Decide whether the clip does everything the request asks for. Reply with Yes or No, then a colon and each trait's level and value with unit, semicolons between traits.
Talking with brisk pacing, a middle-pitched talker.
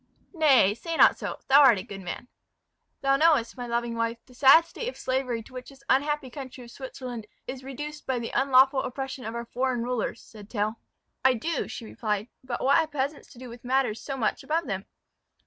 No: fast, 210 wpm; very high, 255 Hz